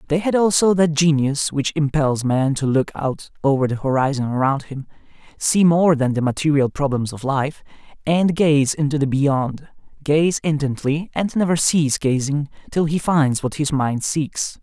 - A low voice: No, medium, 145 Hz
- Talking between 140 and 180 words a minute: Yes, average, 170 wpm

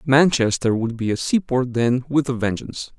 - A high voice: No, low, 125 Hz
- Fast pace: No, average, 180 wpm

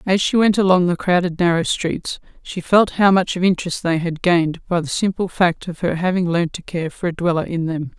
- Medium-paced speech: No, fast, 240 wpm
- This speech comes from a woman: Yes, female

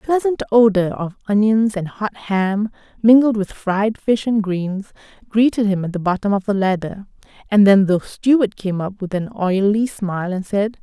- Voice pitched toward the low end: No, high, 205 Hz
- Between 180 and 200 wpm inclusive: Yes, average, 190 wpm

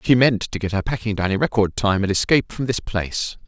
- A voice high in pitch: No, low, 110 Hz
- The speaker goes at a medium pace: No, fast, 260 wpm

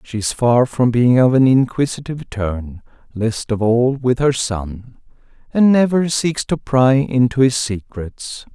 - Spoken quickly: No, average, 145 wpm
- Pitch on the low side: Yes, low, 125 Hz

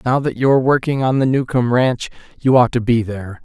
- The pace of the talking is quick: Yes, fast, 225 wpm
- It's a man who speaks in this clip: Yes, male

